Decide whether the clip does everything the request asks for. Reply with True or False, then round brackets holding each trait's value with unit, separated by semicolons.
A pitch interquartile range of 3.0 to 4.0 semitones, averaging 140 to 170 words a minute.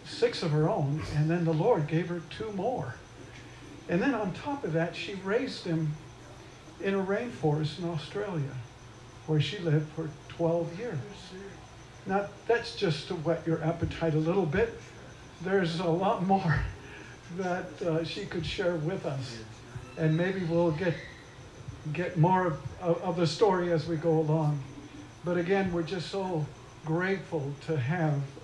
True (3.4 semitones; 160 wpm)